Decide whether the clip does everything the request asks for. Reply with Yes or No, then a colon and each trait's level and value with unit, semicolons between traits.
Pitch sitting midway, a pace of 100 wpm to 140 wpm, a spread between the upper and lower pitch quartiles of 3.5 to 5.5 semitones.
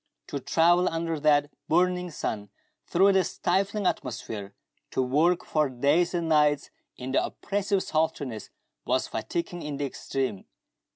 Yes: medium, 155 Hz; slow, 135 wpm; average, 4.5 semitones